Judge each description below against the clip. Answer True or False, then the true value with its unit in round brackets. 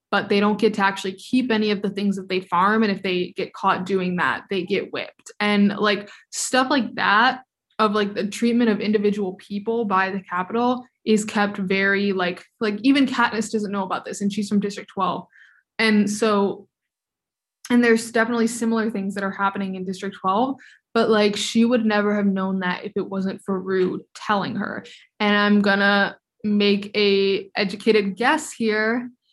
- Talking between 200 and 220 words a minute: False (185 wpm)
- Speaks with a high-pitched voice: True (205 Hz)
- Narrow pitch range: True (2.2 semitones)